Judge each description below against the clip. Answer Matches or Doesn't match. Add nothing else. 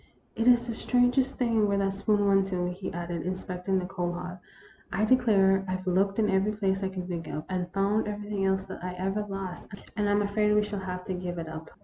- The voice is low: Doesn't match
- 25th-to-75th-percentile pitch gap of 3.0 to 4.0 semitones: Doesn't match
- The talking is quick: Matches